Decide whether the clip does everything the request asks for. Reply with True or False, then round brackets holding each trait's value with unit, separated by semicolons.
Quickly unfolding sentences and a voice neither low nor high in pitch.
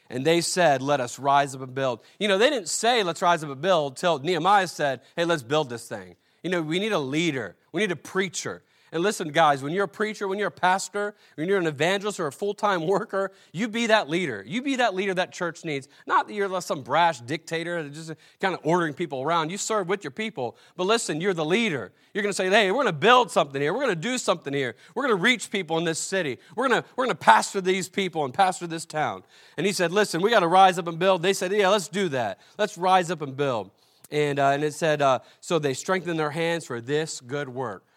True (260 wpm; 175 Hz)